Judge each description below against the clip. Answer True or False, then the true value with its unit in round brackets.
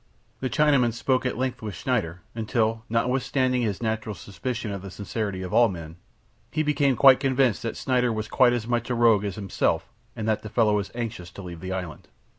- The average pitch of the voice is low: True (115 Hz)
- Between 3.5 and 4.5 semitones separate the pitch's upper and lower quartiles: True (3.8 semitones)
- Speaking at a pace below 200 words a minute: False (205 wpm)